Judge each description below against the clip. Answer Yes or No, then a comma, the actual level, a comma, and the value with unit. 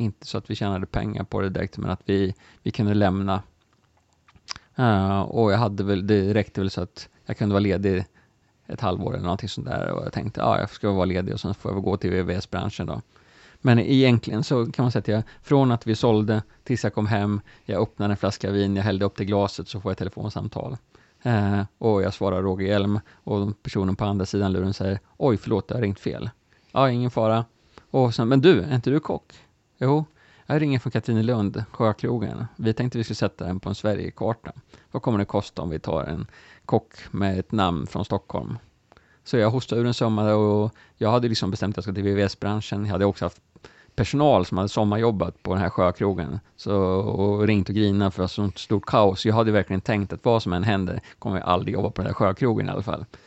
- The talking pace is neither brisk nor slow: No, fast, 230 wpm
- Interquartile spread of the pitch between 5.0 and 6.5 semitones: No, average, 2.9 semitones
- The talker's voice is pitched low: Yes, low, 105 Hz